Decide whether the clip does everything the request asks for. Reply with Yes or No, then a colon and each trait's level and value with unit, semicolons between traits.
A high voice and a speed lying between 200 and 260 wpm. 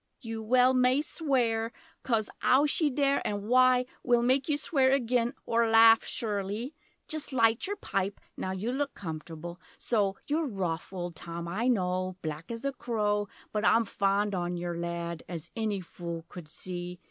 No: high, 220 Hz; average, 170 wpm